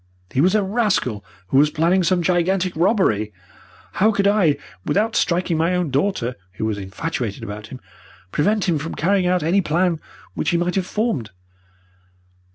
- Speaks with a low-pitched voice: No, medium, 175 Hz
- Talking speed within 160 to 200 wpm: Yes, average, 165 wpm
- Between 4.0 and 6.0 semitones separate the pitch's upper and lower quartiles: Yes, wide, 5.4 semitones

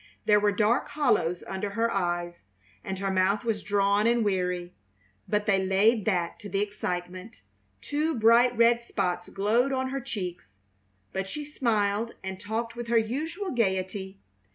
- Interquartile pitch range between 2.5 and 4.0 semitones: Yes, average, 3.6 semitones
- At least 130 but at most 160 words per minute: Yes, average, 155 wpm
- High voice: Yes, high, 205 Hz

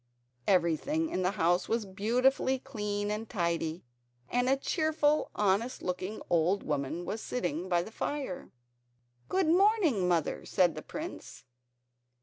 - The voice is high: Yes, high, 205 Hz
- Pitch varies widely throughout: Yes, wide, 7.1 semitones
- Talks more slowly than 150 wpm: Yes, slow, 135 wpm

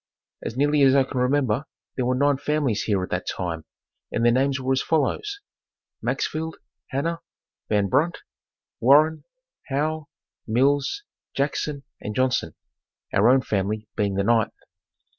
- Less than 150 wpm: Yes, average, 140 wpm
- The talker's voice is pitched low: Yes, low, 130 Hz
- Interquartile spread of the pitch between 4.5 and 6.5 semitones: Yes, average, 4.8 semitones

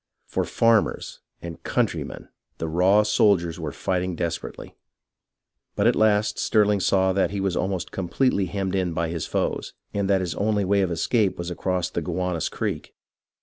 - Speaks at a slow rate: No, average, 175 wpm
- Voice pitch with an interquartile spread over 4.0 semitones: No, average, 2.7 semitones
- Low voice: Yes, very low, 95 Hz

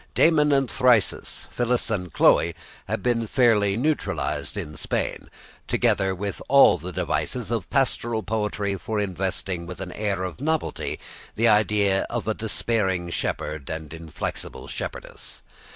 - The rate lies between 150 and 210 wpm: No, slow, 135 wpm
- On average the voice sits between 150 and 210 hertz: No, low, 105 Hz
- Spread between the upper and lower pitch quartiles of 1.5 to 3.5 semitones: No, average, 4.4 semitones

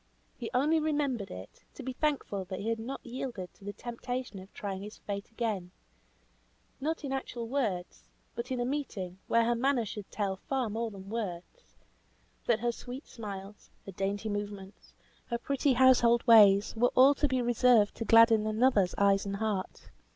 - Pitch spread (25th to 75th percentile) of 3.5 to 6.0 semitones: Yes, average, 4.0 semitones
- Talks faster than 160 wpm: Yes, average, 175 wpm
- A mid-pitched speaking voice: No, high, 230 Hz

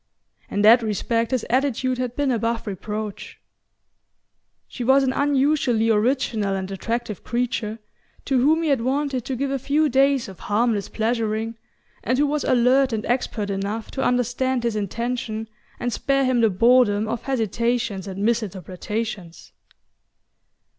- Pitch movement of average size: Yes, average, 3.3 semitones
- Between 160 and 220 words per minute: No, average, 145 wpm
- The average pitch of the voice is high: Yes, high, 235 Hz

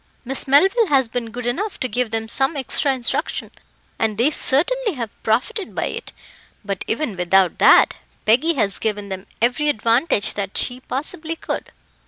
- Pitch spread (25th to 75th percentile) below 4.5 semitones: No, average, 5.3 semitones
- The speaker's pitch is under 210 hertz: No, very high, 250 Hz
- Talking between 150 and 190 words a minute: Yes, average, 165 wpm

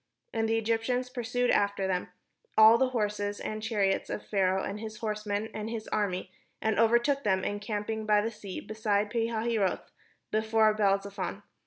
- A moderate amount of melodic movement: No, narrow, 1.7 semitones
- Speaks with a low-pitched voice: No, high, 215 Hz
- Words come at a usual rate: Yes, average, 165 wpm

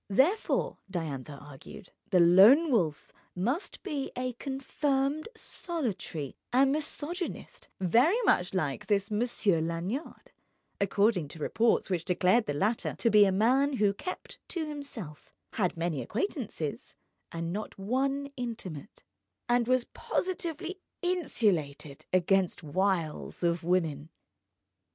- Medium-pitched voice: No, high, 205 Hz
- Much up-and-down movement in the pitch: Yes, wide, 8.0 semitones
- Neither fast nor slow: No, slow, 115 wpm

